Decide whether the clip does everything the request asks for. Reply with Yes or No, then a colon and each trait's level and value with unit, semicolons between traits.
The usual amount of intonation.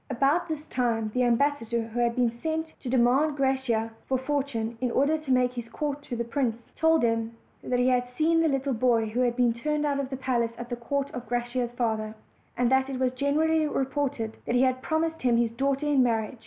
Yes: average, 3.1 semitones